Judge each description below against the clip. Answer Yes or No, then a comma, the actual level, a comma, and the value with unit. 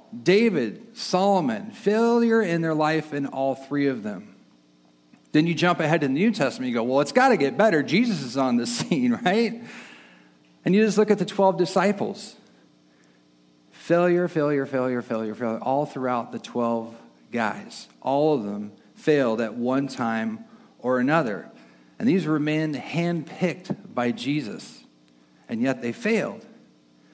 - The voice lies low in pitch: No, medium, 145 Hz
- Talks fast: No, average, 155 wpm